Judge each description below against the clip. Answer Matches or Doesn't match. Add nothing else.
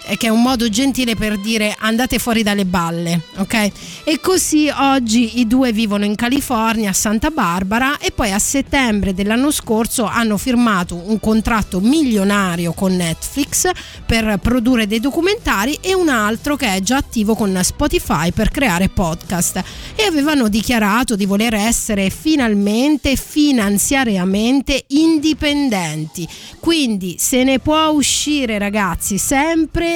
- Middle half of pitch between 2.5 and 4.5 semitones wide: Doesn't match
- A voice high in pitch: Matches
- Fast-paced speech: Doesn't match